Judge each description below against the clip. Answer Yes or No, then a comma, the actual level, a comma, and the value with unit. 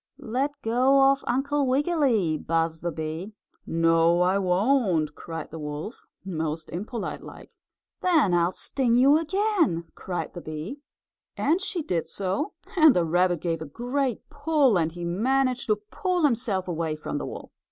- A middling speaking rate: Yes, average, 155 wpm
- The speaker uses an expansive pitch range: Yes, wide, 8.6 semitones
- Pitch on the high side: Yes, high, 205 Hz